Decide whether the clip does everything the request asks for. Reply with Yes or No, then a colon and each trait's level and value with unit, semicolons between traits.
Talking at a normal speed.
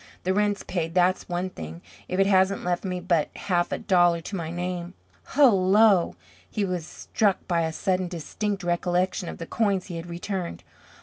Yes: average, 180 wpm